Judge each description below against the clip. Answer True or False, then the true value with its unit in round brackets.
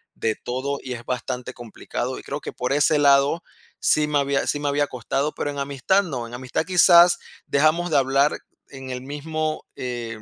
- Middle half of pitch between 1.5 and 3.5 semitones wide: True (2.9 semitones)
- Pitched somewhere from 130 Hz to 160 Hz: True (140 Hz)